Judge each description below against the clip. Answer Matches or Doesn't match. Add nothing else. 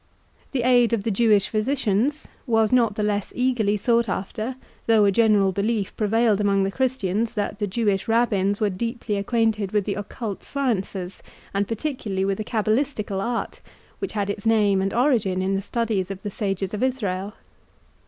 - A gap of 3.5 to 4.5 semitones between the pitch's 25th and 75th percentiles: Doesn't match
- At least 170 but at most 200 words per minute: Matches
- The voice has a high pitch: Matches